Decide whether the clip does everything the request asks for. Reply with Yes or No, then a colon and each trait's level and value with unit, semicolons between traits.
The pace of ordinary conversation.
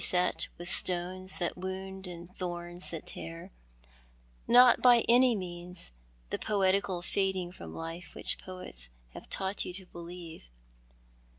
No: slow, 130 wpm